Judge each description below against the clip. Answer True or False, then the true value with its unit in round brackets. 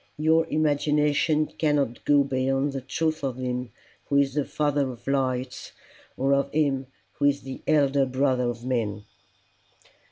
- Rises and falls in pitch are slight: True (2.2 semitones)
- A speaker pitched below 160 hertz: True (140 Hz)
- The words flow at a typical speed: True (150 wpm)